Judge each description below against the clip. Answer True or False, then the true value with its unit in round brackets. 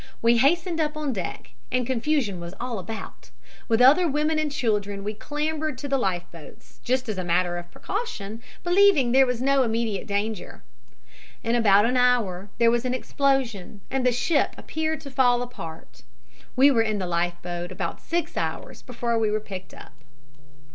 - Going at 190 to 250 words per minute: False (180 wpm)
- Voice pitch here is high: True (240 Hz)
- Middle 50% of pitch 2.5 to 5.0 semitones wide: False (5.5 semitones)